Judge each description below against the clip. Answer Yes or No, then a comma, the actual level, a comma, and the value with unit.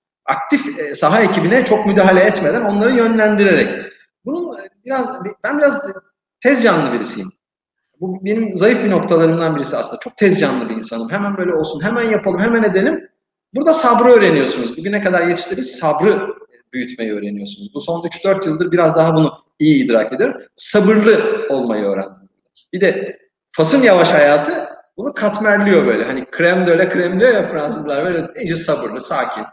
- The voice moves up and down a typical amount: No, wide, 6.3 semitones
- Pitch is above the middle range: Yes, high, 195 Hz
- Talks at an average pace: No, fast, 155 wpm